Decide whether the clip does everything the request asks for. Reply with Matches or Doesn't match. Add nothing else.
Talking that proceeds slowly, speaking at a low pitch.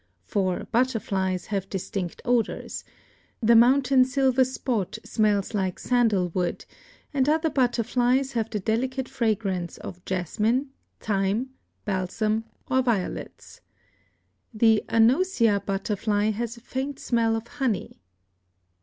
Doesn't match